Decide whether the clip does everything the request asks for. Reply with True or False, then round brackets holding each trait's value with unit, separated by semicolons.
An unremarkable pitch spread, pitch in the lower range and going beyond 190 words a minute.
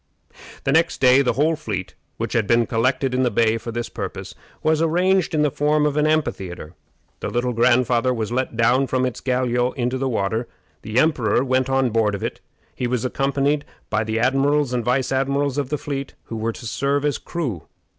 True (3.3 semitones; 130 Hz; 205 wpm)